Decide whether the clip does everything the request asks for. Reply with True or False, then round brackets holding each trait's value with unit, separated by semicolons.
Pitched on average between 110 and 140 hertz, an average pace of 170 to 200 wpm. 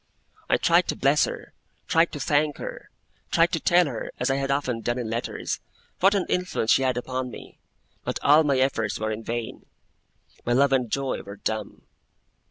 True (135 Hz; 190 wpm)